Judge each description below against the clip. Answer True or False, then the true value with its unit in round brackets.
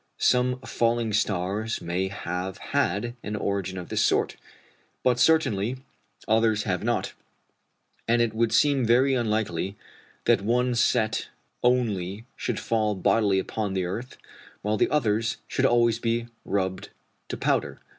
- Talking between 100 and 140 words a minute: True (135 wpm)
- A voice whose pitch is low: True (110 Hz)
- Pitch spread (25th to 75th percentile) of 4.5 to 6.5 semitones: False (3.3 semitones)